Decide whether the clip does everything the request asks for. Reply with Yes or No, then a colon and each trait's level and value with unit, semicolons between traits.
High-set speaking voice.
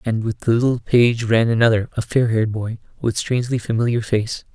No: low, 115 Hz